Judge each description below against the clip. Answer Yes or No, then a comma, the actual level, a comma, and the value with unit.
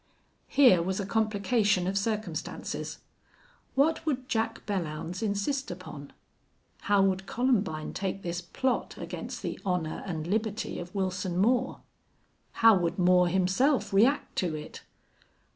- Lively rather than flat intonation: No, average, 4.0 semitones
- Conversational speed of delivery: No, slow, 125 wpm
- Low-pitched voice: No, high, 195 Hz